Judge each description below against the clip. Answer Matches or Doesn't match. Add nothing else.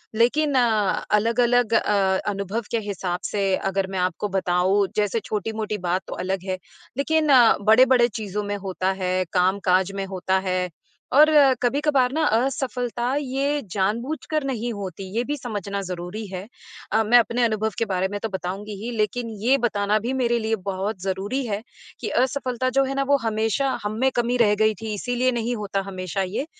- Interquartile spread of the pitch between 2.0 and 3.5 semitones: Doesn't match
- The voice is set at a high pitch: Matches